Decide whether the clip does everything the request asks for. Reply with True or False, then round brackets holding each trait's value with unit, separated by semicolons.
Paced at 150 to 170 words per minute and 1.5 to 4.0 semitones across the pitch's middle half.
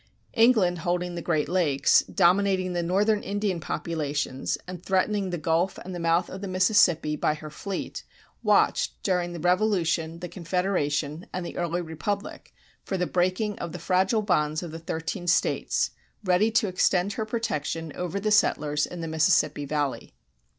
True (165 wpm; 3.0 semitones)